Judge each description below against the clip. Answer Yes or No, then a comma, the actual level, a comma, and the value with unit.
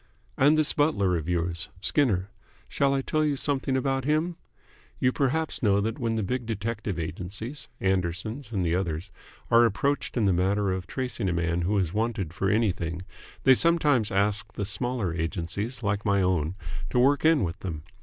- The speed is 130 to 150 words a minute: No, average, 180 wpm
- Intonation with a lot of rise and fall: Yes, wide, 6.1 semitones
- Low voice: Yes, low, 105 Hz